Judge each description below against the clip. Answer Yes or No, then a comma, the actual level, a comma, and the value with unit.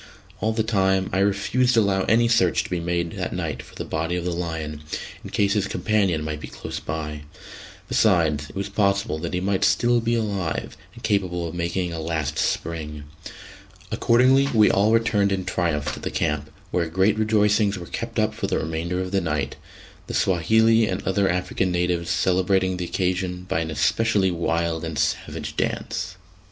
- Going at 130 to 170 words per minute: No, average, 185 wpm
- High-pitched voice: No, very low, 90 Hz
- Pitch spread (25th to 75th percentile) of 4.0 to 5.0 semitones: No, average, 3.5 semitones